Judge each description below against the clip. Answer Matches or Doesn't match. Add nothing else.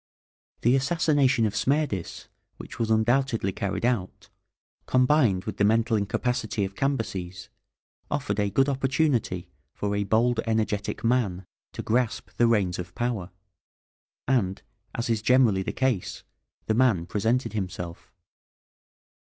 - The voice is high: Doesn't match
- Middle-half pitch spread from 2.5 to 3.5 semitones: Doesn't match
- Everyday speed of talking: Doesn't match